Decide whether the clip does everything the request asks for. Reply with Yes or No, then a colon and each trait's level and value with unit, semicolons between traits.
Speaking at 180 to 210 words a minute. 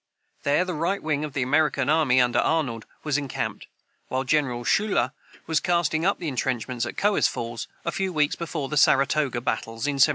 Yes: average, 185 wpm